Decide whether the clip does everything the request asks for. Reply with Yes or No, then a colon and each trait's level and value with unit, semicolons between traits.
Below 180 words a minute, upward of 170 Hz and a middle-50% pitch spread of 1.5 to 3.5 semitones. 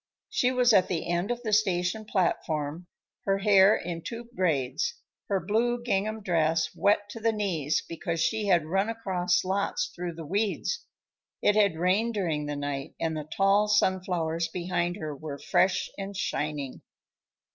No: average, 160 wpm; medium, 185 Hz; average, 4.3 semitones